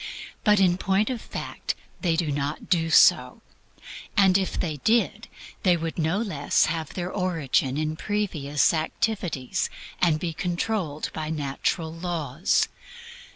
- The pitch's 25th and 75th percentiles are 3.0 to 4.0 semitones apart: Yes, average, 3.5 semitones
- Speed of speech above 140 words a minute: No, slow, 135 wpm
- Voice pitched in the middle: Yes, medium, 165 Hz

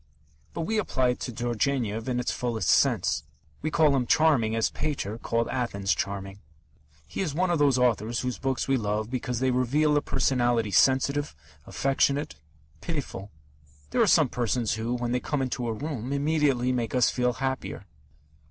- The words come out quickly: No, average, 170 wpm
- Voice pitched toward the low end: Yes, low, 125 Hz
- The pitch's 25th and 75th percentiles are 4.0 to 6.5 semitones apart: No, average, 3.3 semitones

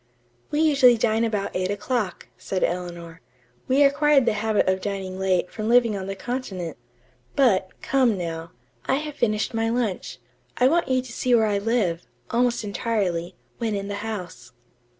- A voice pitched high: Yes, high, 215 Hz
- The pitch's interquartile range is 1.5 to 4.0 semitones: No, average, 4.7 semitones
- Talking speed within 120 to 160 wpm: No, average, 170 wpm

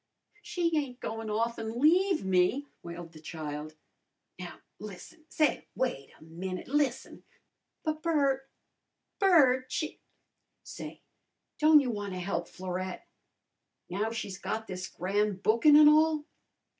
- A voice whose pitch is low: No, high, 225 Hz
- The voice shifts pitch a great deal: Yes, wide, 8.4 semitones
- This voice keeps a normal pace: No, slow, 130 wpm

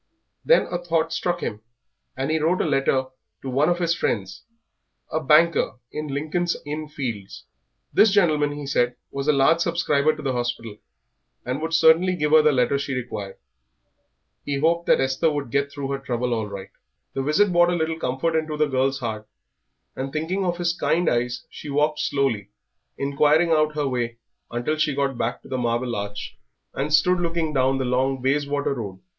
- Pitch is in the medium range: Yes, medium, 145 Hz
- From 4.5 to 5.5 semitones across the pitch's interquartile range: No, average, 3.9 semitones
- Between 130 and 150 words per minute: No, average, 185 wpm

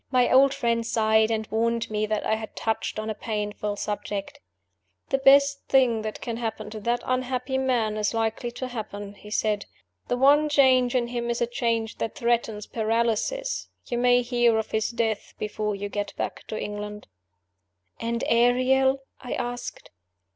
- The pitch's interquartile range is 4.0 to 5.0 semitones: No, narrow, 2.6 semitones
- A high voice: Yes, high, 230 Hz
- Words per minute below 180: Yes, average, 170 wpm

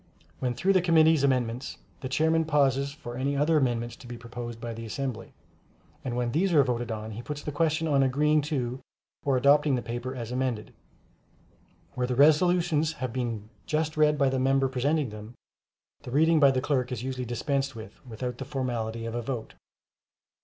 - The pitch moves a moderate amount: Yes, average, 3.7 semitones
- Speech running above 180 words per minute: Yes, average, 190 wpm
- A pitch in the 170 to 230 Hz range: No, low, 130 Hz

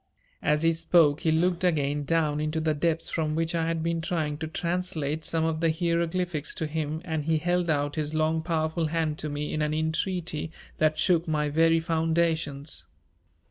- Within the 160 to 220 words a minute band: Yes, average, 185 wpm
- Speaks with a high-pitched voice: No, medium, 160 Hz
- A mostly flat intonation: Yes, narrow, 1.4 semitones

